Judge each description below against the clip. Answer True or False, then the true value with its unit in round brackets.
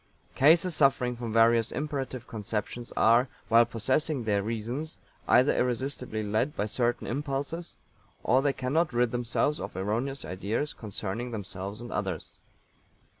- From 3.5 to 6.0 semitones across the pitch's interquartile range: True (3.8 semitones)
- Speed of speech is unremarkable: False (130 wpm)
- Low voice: True (120 Hz)